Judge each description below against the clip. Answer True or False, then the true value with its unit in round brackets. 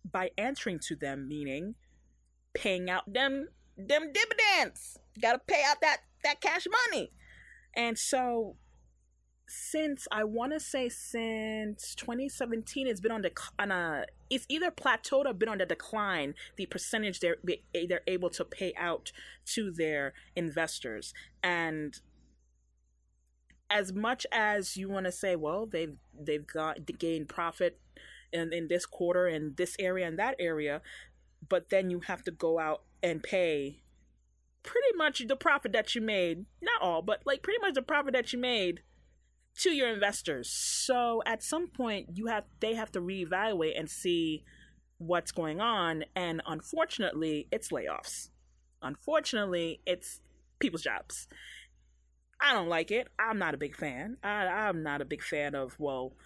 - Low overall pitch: False (185 Hz)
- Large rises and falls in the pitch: True (7.5 semitones)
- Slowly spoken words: False (160 wpm)